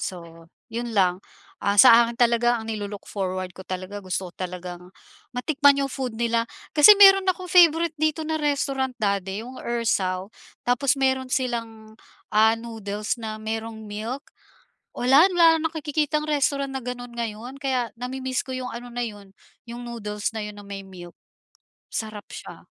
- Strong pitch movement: No, average, 4.4 semitones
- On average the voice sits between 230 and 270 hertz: Yes, high, 235 Hz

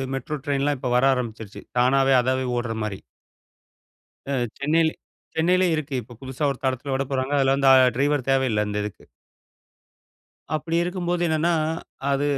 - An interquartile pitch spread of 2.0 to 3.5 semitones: Yes, average, 3.2 semitones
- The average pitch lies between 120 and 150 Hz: Yes, low, 135 Hz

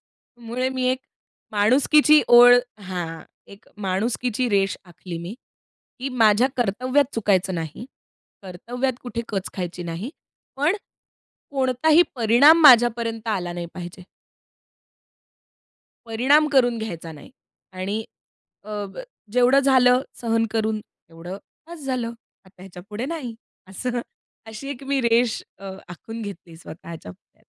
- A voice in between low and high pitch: No, high, 230 Hz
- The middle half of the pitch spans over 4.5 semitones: Yes, average, 5.1 semitones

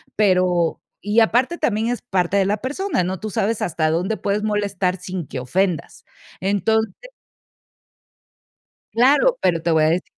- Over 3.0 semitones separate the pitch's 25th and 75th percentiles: Yes, average, 3.7 semitones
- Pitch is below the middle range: No, high, 200 Hz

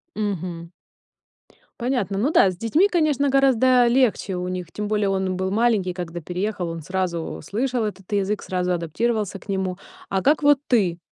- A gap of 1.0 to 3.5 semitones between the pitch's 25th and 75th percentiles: No, average, 4.8 semitones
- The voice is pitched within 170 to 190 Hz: No, high, 200 Hz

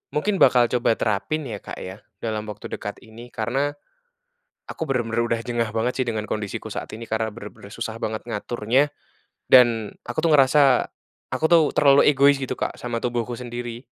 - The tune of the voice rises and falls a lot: No, average, 2.7 semitones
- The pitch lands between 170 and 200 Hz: No, low, 120 Hz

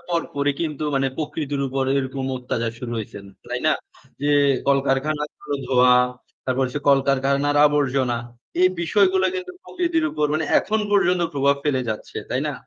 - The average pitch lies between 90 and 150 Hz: Yes, medium, 140 Hz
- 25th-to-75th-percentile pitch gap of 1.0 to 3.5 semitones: Yes, average, 2.8 semitones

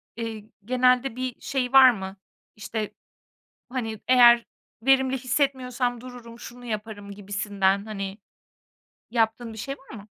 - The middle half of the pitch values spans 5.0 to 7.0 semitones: No, average, 3.2 semitones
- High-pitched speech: Yes, high, 235 Hz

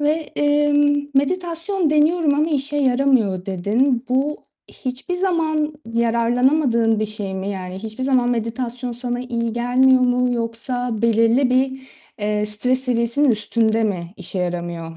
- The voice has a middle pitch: No, high, 245 Hz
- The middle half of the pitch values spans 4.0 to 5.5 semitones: Yes, average, 4.3 semitones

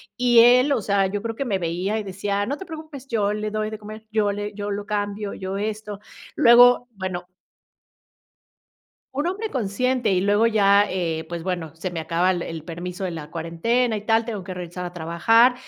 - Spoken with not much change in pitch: No, average, 4.0 semitones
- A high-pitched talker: Yes, high, 205 Hz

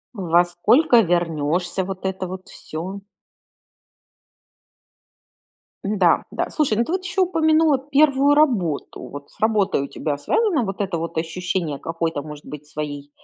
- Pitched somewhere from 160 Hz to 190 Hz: Yes, medium, 185 Hz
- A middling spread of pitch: No, wide, 8.5 semitones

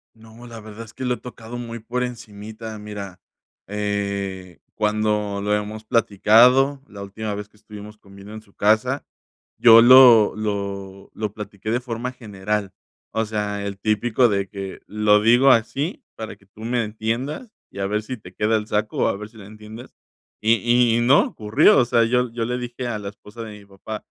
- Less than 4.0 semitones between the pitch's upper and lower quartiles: Yes, narrow, 2.4 semitones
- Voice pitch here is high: No, low, 110 Hz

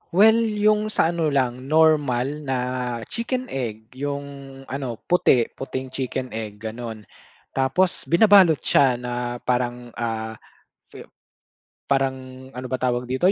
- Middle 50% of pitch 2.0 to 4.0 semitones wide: No, average, 4.8 semitones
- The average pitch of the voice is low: Yes, low, 130 Hz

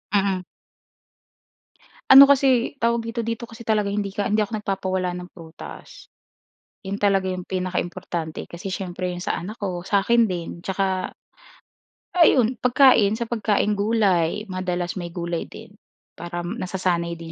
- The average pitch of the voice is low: No, high, 195 Hz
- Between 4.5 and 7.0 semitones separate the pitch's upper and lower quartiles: No, average, 3.7 semitones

